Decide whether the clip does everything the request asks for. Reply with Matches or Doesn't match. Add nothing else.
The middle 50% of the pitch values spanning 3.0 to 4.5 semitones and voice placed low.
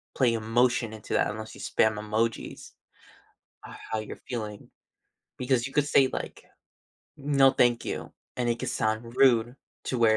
Doesn't match